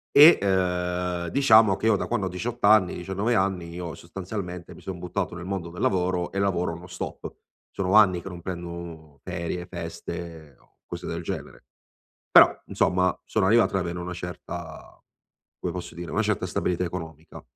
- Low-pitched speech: Yes, very low, 90 Hz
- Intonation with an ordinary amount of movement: No, narrow, 1.9 semitones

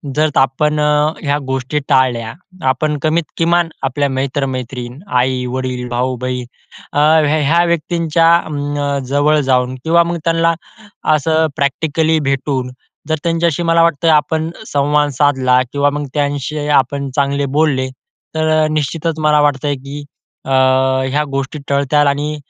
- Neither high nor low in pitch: Yes, medium, 145 Hz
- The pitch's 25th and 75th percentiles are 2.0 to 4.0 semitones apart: Yes, average, 2.8 semitones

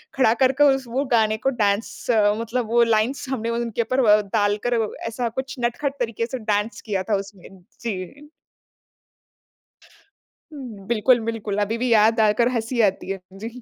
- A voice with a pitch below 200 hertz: No, high, 230 Hz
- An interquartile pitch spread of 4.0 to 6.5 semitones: No, narrow, 2.6 semitones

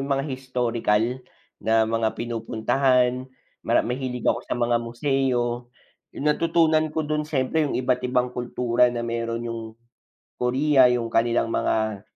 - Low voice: Yes, low, 125 Hz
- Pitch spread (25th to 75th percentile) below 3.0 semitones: Yes, narrow, 2.4 semitones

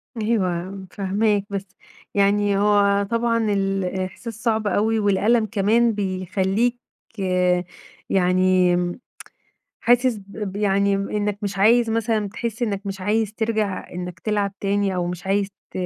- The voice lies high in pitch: Yes, high, 200 Hz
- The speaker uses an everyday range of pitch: No, narrow, 2.3 semitones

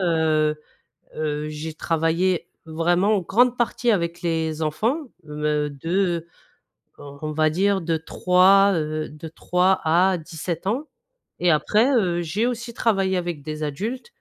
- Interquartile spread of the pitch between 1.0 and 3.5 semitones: No, average, 3.9 semitones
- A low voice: No, medium, 170 Hz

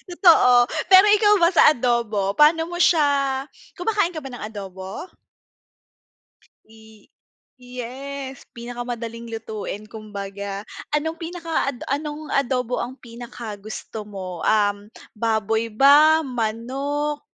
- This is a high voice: Yes, high, 245 Hz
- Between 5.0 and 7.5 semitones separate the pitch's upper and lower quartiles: Yes, average, 5.3 semitones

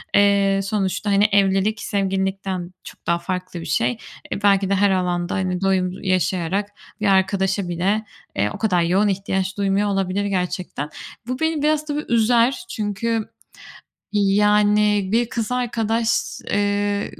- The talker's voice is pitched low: No, high, 200 Hz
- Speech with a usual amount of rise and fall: No, narrow, 2.0 semitones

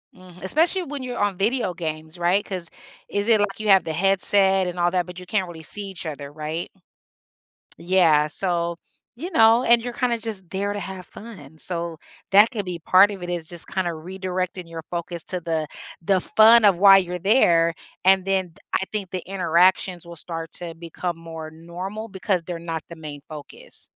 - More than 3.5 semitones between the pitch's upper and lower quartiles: No, average, 2.9 semitones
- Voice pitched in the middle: Yes, medium, 180 Hz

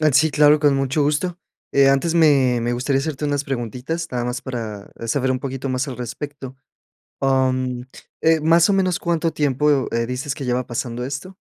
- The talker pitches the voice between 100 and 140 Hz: Yes, low, 135 Hz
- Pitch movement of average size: Yes, average, 3.1 semitones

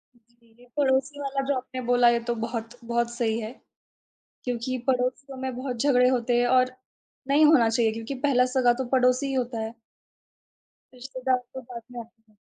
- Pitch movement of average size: No, narrow, 1.8 semitones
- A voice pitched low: No, very high, 250 Hz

